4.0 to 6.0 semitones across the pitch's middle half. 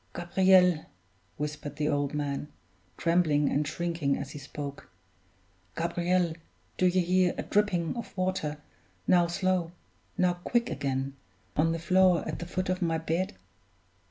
No: average, 3.6 semitones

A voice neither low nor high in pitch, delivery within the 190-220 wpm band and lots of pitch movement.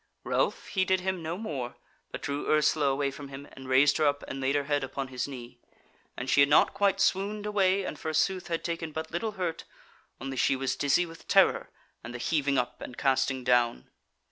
No: medium, 145 Hz; fast, 205 wpm; average, 4.3 semitones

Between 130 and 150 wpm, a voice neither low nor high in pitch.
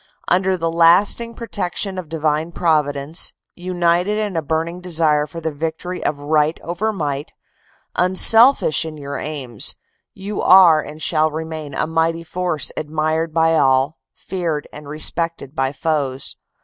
Yes: average, 140 wpm; medium, 160 Hz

